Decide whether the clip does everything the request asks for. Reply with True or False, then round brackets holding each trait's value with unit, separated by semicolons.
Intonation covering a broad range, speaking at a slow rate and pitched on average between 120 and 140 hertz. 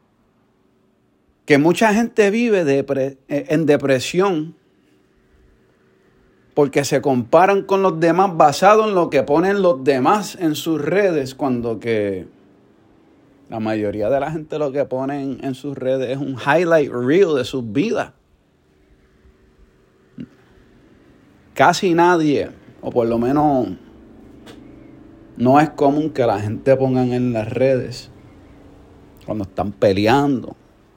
True (6.4 semitones; 120 wpm; 135 Hz)